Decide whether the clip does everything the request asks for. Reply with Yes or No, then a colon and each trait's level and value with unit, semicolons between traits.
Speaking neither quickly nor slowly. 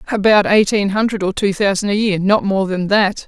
No: fast, 220 wpm